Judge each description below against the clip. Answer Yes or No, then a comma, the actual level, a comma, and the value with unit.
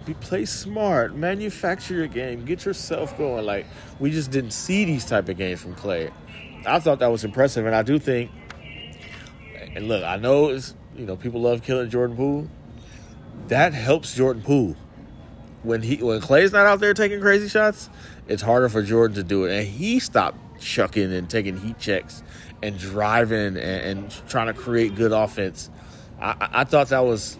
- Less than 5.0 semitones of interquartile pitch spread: No, wide, 5.5 semitones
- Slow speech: No, average, 185 wpm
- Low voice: Yes, low, 120 Hz